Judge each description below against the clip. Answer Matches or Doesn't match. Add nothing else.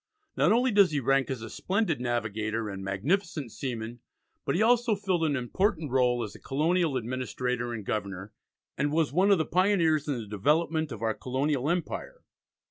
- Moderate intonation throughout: Doesn't match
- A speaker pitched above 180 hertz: Doesn't match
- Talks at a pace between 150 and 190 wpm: Matches